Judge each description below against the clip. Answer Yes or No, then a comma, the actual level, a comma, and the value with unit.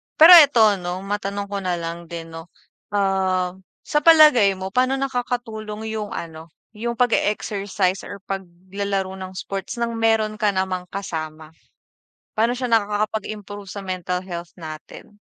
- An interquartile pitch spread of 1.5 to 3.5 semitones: Yes, average, 3.2 semitones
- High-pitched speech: Yes, high, 200 Hz